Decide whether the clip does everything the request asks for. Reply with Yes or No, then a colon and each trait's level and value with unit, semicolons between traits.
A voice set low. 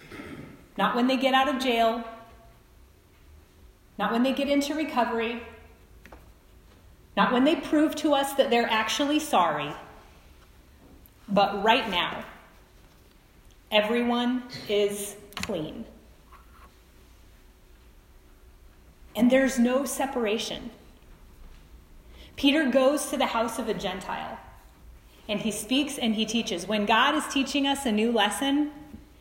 No: high, 220 Hz